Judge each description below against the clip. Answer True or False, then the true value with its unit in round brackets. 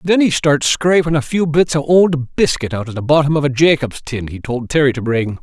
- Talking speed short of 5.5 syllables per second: True (5.3 syllables/s)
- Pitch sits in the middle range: True (145 Hz)